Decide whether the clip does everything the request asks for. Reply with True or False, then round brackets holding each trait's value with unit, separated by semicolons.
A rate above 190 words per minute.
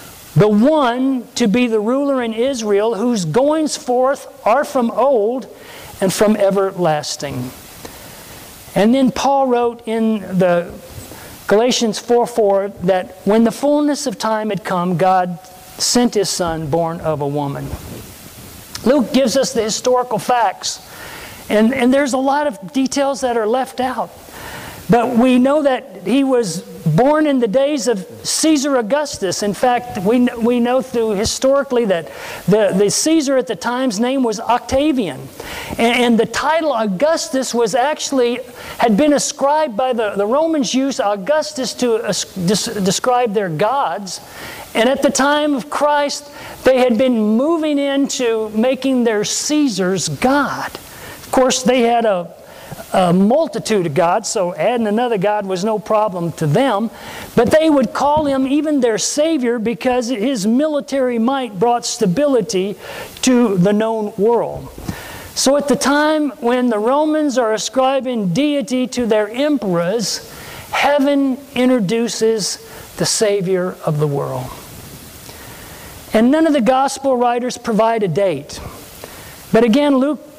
False (145 wpm)